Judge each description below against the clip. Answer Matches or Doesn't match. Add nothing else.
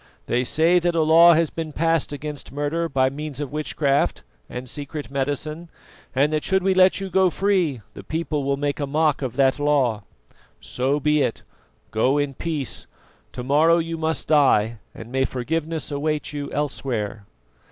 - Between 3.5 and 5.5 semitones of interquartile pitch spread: Doesn't match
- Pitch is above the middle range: Doesn't match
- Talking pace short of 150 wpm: Doesn't match